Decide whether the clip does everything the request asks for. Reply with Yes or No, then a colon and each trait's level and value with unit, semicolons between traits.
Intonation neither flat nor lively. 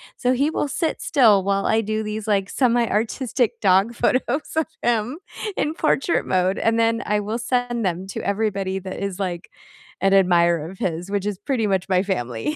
Yes: average, 4.0 semitones